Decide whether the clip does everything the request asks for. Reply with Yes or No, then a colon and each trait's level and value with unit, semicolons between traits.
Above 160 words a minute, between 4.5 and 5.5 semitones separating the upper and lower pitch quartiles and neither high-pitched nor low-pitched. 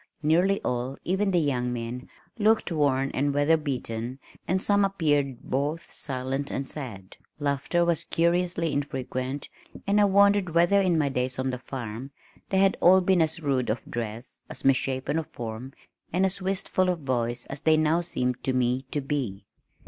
Yes: average, 170 wpm; average, 5.2 semitones; medium, 145 Hz